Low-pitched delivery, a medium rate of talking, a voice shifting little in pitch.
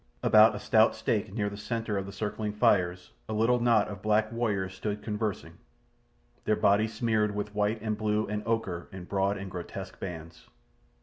Yes: low, 105 Hz; average, 180 wpm; narrow, 1.9 semitones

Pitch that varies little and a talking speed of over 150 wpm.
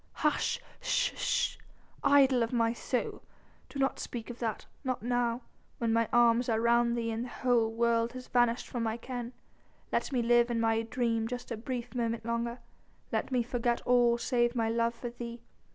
Yes: narrow, 1.1 semitones; average, 185 wpm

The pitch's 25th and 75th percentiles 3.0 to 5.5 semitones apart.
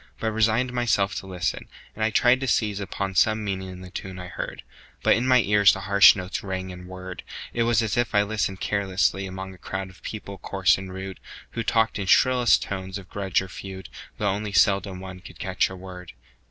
No: narrow, 2.4 semitones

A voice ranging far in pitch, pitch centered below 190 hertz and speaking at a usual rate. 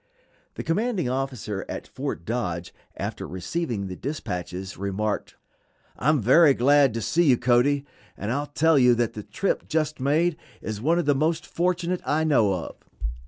Yes: wide, 6.9 semitones; low, 135 Hz; average, 165 wpm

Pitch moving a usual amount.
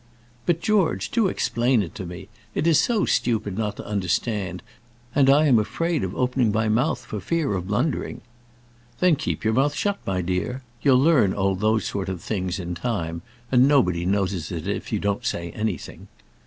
No: wide, 6.6 semitones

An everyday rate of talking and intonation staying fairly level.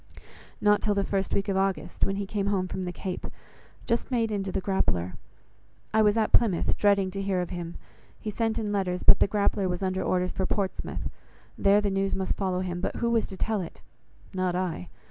No: fast, 215 wpm; narrow, 1.9 semitones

